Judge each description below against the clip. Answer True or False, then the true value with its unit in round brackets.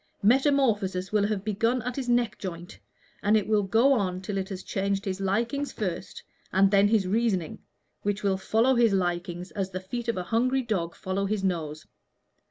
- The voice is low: False (200 Hz)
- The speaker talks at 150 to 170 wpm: False (185 wpm)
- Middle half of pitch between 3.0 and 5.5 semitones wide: True (3.5 semitones)